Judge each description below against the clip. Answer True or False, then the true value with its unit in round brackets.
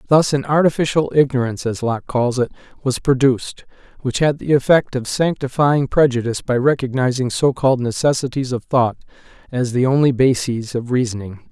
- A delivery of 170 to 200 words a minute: False (150 wpm)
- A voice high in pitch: False (130 Hz)